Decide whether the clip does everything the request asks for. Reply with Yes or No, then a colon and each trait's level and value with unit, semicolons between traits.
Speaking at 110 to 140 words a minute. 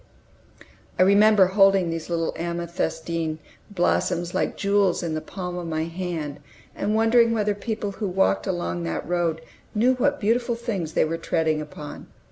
No: average, 155 wpm